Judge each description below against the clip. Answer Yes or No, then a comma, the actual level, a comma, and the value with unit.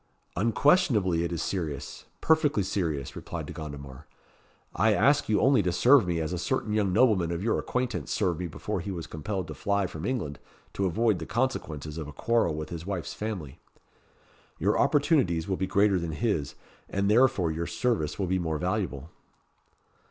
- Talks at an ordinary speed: Yes, average, 180 wpm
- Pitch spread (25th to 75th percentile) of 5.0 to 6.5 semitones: Yes, average, 5.3 semitones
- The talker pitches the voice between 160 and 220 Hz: No, very low, 95 Hz